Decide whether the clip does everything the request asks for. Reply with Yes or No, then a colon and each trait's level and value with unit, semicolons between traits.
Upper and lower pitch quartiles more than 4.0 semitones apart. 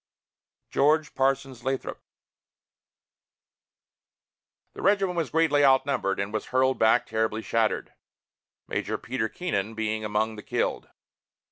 Yes: average, 4.5 semitones